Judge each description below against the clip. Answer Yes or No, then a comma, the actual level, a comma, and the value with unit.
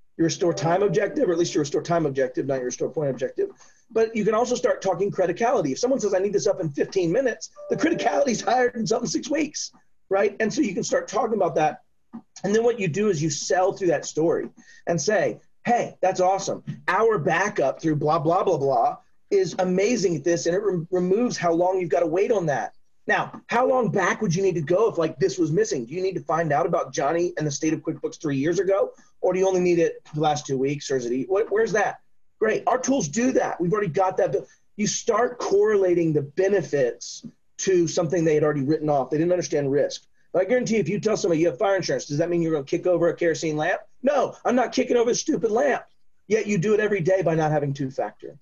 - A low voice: No, high, 190 Hz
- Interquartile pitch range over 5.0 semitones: Yes, wide, 5.4 semitones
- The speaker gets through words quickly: Yes, fast, 250 wpm